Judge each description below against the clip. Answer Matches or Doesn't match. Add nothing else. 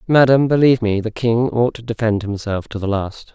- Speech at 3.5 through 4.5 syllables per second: Doesn't match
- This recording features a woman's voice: Doesn't match